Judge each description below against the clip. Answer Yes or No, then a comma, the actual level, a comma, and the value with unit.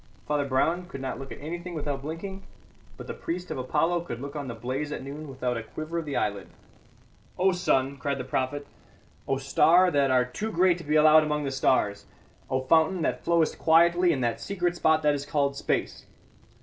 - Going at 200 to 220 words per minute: Yes, fast, 205 wpm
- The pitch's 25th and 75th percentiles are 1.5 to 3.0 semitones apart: No, average, 4.0 semitones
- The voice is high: No, medium, 150 Hz